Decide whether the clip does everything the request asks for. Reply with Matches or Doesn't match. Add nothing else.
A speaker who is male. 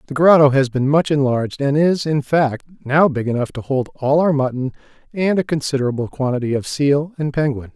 Matches